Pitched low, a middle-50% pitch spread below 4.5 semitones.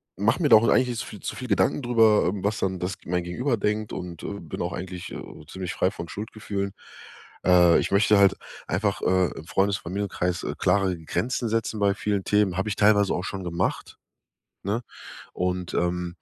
Yes: low, 100 Hz; narrow, 2.6 semitones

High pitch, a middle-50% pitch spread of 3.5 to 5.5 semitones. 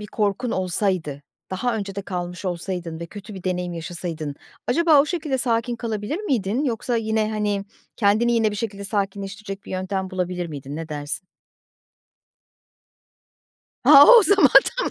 Yes: high, 200 Hz; average, 4.3 semitones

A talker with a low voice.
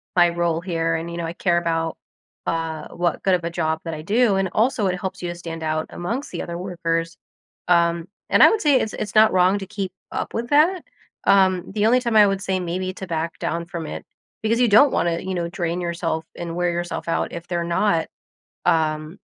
No: medium, 175 Hz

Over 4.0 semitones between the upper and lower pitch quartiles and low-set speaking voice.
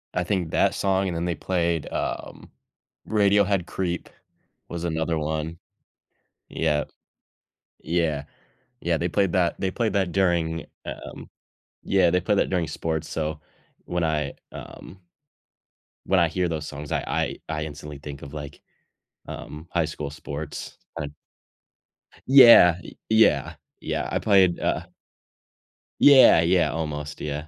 No: average, 3.5 semitones; very low, 85 Hz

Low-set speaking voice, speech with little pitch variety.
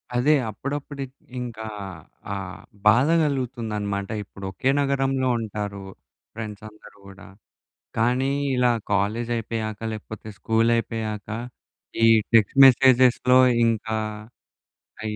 No: low, 115 Hz; average, 3.3 semitones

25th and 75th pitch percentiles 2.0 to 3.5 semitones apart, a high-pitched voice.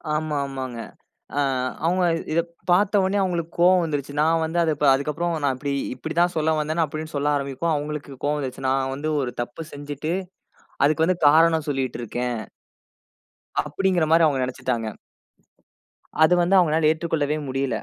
No: average, 3.2 semitones; medium, 155 Hz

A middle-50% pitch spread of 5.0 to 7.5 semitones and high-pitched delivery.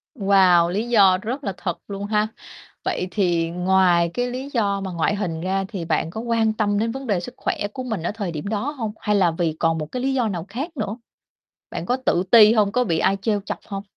No: average, 4.1 semitones; high, 200 Hz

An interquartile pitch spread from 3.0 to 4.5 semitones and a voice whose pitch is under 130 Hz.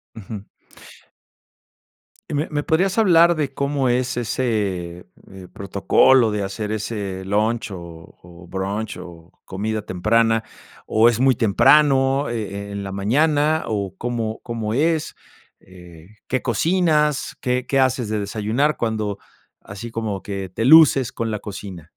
No: average, 5.0 semitones; low, 110 Hz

